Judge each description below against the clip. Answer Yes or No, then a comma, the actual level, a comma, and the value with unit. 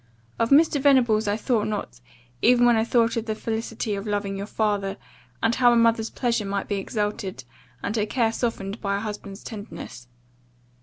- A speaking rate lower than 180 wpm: No, average, 185 wpm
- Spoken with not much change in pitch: Yes, narrow, 2.3 semitones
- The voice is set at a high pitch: Yes, high, 220 Hz